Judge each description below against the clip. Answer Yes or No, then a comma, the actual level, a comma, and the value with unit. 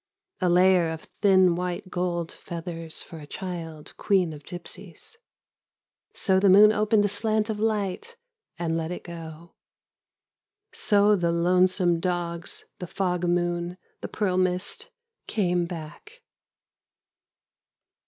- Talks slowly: Yes, slow, 125 wpm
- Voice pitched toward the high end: No, medium, 180 Hz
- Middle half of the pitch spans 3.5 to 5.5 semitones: No, average, 2.7 semitones